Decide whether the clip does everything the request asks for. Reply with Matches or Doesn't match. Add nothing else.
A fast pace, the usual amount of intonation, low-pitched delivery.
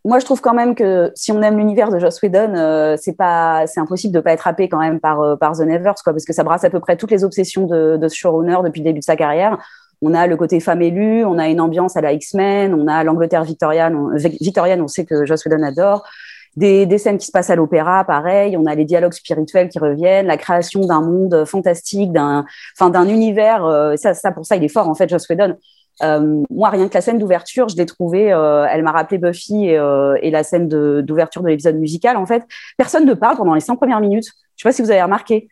Doesn't match